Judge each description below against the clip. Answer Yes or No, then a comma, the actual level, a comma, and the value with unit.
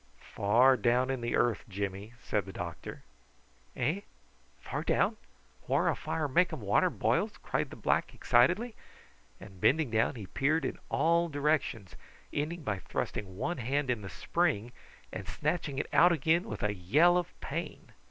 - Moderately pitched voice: No, low, 130 Hz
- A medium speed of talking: Yes, average, 160 wpm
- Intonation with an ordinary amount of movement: No, wide, 7.4 semitones